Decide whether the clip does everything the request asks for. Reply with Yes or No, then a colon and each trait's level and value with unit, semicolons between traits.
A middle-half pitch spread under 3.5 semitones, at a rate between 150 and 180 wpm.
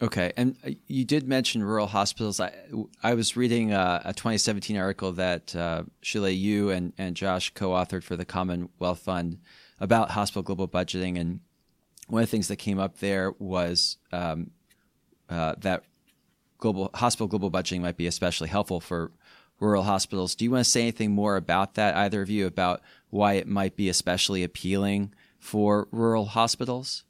Yes: average, 3.0 semitones; average, 170 wpm